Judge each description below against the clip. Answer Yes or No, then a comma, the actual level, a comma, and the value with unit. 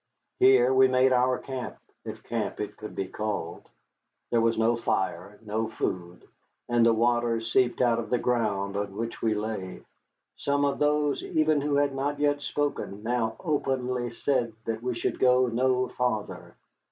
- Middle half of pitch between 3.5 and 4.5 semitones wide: No, average, 3.0 semitones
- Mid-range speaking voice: No, low, 120 Hz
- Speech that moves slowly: No, average, 165 wpm